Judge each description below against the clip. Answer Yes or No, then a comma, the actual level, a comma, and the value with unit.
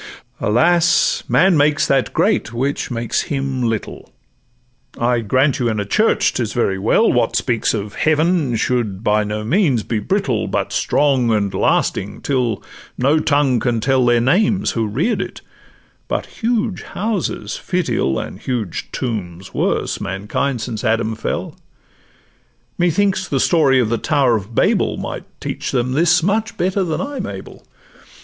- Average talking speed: Yes, average, 150 wpm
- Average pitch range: No, wide, 6.6 semitones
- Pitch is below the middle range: Yes, low, 130 Hz